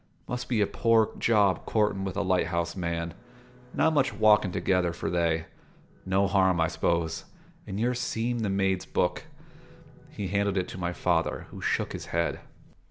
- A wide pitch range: No, average, 3.8 semitones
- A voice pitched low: Yes, very low, 95 Hz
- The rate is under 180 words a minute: Yes, average, 170 wpm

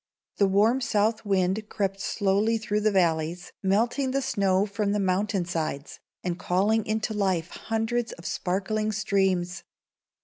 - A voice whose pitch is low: No, high, 200 Hz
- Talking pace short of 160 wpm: Yes, average, 140 wpm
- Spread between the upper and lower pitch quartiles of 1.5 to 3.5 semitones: Yes, average, 2.7 semitones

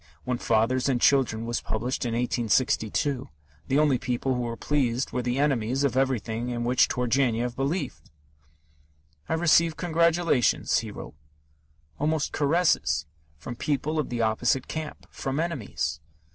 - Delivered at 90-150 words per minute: Yes, average, 140 wpm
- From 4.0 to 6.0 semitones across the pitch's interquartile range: No, average, 3.6 semitones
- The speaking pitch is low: Yes, low, 130 Hz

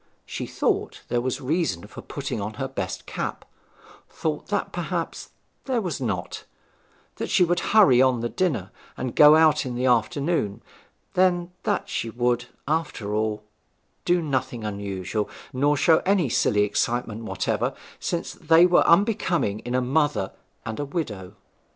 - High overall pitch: No, low, 130 Hz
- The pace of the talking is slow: No, average, 150 wpm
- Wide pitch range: Yes, wide, 6.9 semitones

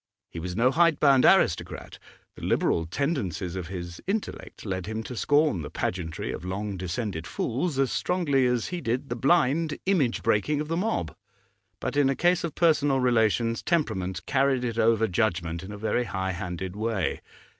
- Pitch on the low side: Yes, low, 115 Hz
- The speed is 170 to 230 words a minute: Yes, average, 175 wpm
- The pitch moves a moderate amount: No, wide, 7.4 semitones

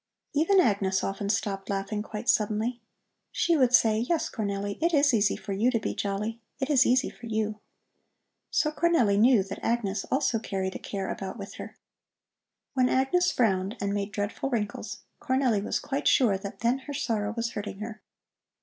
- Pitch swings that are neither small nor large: Yes, average, 4.4 semitones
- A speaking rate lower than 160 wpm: No, average, 175 wpm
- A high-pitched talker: Yes, high, 220 Hz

